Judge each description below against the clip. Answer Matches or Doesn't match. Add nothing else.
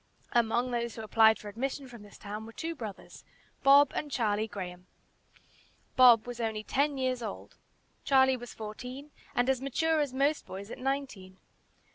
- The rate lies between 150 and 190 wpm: Matches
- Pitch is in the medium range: Doesn't match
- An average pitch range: Matches